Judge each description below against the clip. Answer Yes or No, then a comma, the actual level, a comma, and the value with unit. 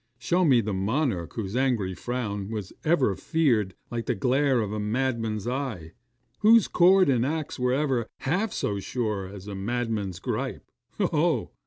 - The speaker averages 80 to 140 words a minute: No, average, 165 wpm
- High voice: No, low, 120 Hz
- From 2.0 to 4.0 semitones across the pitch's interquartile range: No, average, 4.9 semitones